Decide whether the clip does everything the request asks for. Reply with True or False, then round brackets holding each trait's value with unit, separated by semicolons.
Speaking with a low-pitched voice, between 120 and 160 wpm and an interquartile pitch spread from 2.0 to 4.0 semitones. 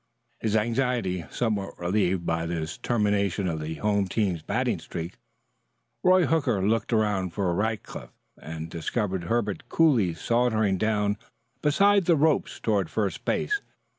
False (105 Hz; 135 wpm; 4.6 semitones)